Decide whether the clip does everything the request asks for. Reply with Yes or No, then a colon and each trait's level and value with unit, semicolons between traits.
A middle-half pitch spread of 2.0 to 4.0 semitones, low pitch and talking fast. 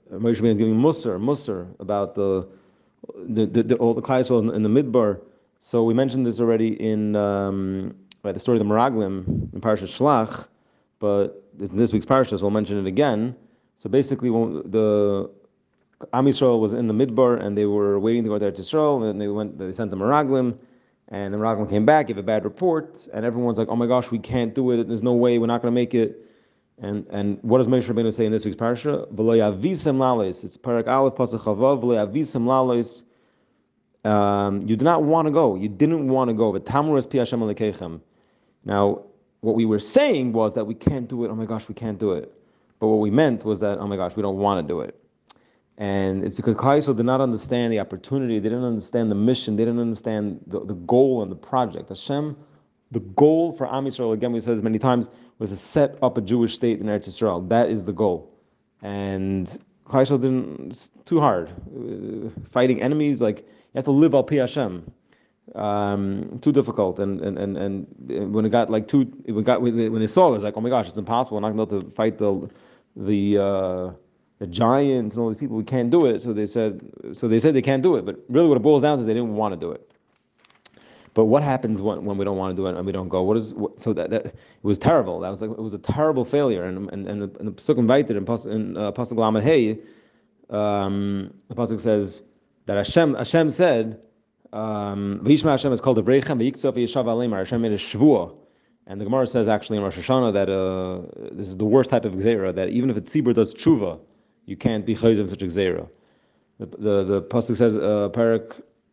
Yes: average, 3.4 semitones; low, 110 Hz; fast, 210 wpm